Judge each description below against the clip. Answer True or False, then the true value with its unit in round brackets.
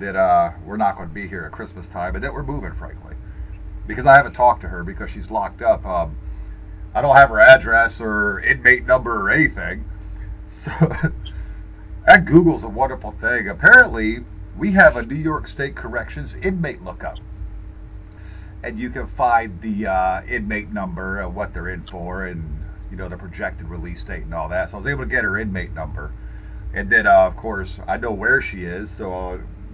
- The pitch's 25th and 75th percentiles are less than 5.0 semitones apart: True (4.5 semitones)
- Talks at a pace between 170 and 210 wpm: True (195 wpm)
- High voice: False (100 Hz)